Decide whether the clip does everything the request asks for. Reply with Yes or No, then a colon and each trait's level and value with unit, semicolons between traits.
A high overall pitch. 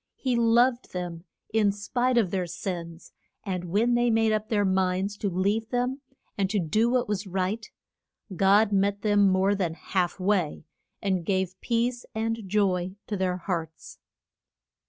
Yes: high, 200 Hz